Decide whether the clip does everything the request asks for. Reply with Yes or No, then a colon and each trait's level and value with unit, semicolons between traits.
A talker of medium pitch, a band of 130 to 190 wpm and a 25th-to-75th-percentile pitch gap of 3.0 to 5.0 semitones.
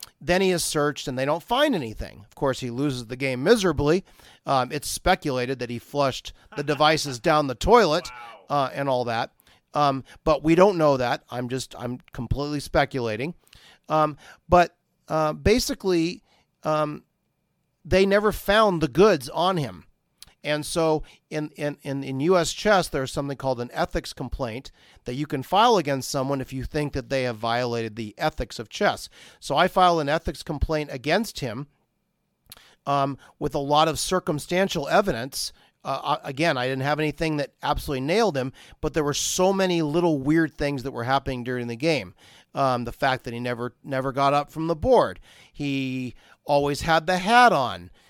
Yes: medium, 145 Hz; average, 175 wpm; average, 3.9 semitones